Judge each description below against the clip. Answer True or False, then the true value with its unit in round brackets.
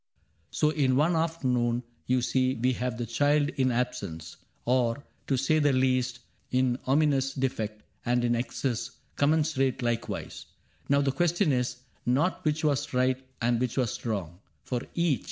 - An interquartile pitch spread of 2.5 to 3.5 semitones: True (2.8 semitones)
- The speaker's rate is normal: True (165 wpm)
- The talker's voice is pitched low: True (130 Hz)